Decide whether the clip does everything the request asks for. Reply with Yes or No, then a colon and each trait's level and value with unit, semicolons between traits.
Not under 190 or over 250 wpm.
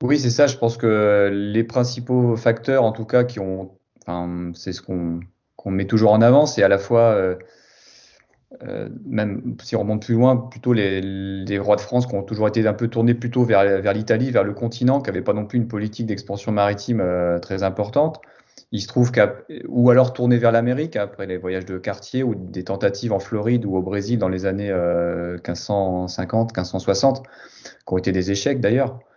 Yes: average, 205 wpm